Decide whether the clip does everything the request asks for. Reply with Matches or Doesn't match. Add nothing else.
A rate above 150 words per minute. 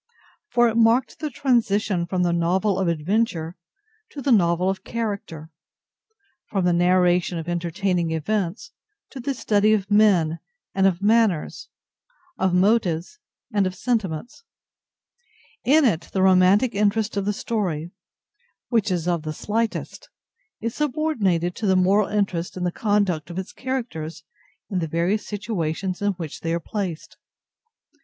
Doesn't match